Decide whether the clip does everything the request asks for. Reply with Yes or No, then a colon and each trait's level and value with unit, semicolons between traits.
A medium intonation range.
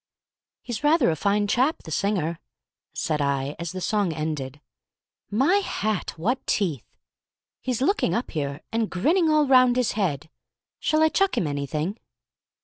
No: wide, 8.5 semitones